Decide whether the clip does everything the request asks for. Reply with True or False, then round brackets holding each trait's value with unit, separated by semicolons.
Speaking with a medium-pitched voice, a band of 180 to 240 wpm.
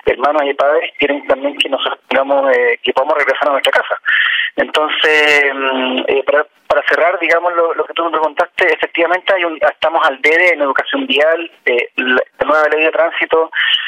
True (165 Hz; 185 wpm)